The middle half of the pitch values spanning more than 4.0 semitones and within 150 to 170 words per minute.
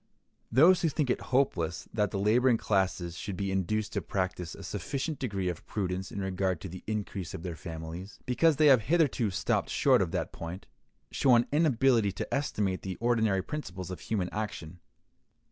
No: wide, 5.4 semitones; average, 180 wpm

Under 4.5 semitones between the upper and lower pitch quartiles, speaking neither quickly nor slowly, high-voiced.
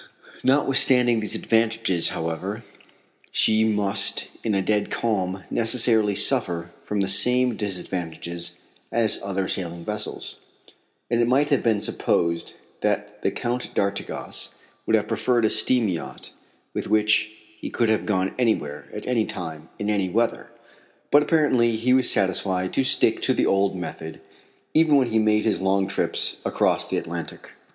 No: average, 3.8 semitones; average, 150 wpm; low, 105 Hz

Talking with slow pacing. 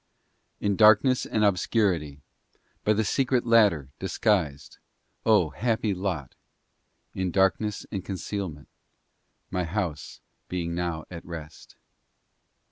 Yes: slow, 110 wpm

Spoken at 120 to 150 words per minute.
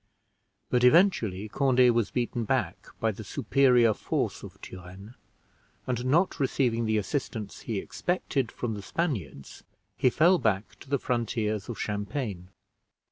Yes: slow, 135 wpm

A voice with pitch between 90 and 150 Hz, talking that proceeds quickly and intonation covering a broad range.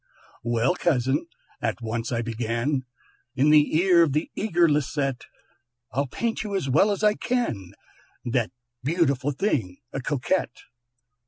No: medium, 140 Hz; average, 140 wpm; wide, 6.1 semitones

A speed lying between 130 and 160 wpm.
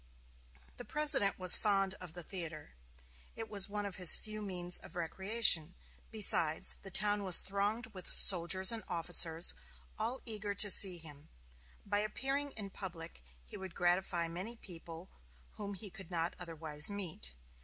Yes: average, 155 wpm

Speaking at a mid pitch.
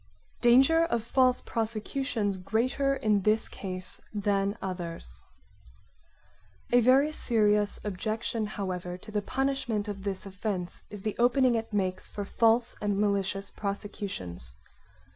No: high, 210 Hz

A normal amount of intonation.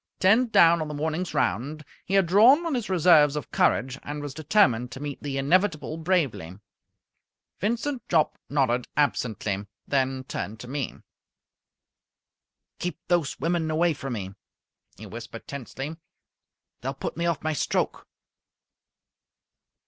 Yes: average, 4.6 semitones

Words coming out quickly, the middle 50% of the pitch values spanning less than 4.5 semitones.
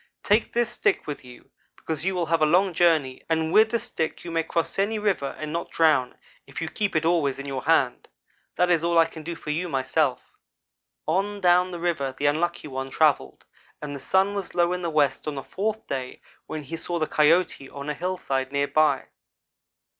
Yes: fast, 215 wpm; average, 4.0 semitones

